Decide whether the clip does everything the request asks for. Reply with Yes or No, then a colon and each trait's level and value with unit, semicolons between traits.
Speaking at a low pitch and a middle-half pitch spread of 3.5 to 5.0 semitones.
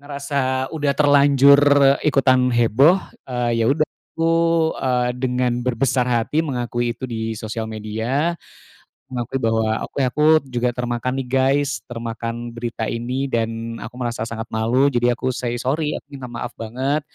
No: low, 125 Hz; average, 2.8 semitones